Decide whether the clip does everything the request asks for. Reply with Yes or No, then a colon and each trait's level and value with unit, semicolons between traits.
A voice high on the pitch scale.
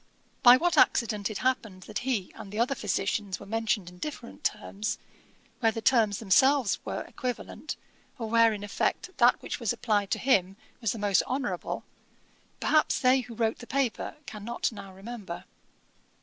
Yes: high, 225 Hz